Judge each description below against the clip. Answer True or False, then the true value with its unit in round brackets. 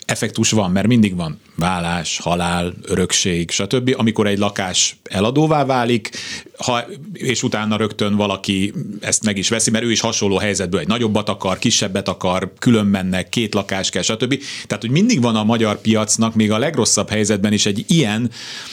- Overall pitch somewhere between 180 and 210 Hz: False (110 Hz)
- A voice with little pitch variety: False (3.0 semitones)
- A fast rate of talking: True (170 wpm)